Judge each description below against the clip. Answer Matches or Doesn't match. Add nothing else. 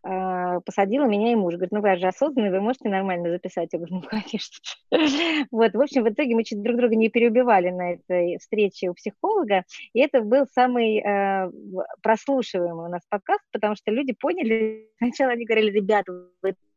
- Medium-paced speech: Doesn't match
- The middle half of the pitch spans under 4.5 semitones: Doesn't match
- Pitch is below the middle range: Doesn't match